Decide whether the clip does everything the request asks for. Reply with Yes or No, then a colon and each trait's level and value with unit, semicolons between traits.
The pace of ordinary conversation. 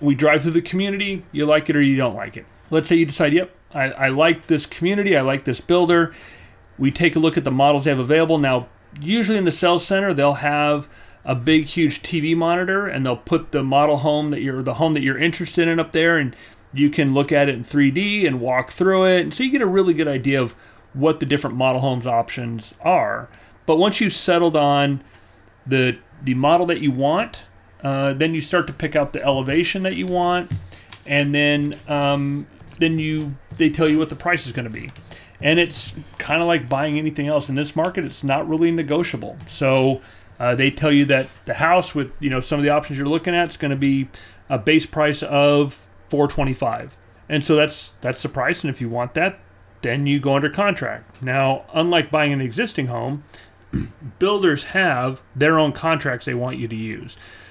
No: fast, 215 wpm